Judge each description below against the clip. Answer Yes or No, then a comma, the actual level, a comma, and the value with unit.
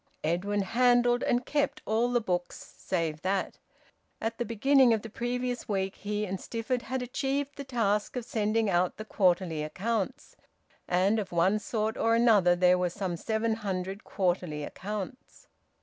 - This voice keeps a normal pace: Yes, average, 160 wpm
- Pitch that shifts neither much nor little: Yes, average, 4.6 semitones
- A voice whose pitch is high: Yes, high, 210 Hz